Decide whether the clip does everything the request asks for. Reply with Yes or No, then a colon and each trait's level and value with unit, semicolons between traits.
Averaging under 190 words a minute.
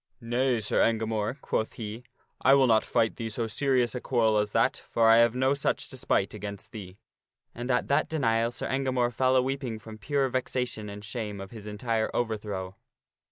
No: fast, 205 wpm